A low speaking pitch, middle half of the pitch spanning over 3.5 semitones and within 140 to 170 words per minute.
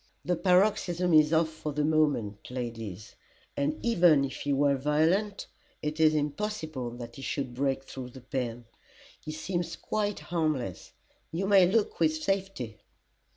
No: medium, 155 Hz; average, 5.0 semitones; average, 150 wpm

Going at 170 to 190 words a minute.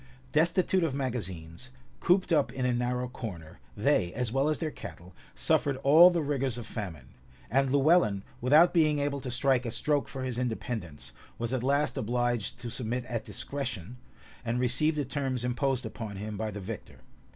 Yes: average, 175 wpm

